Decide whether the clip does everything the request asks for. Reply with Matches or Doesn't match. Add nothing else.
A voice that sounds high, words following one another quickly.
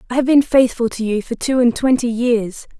Matches